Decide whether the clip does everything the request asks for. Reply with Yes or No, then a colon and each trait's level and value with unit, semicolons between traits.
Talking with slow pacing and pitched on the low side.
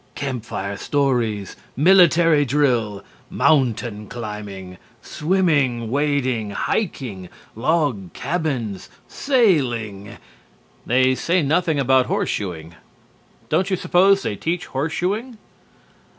Yes: slow, 90 wpm; low, 130 Hz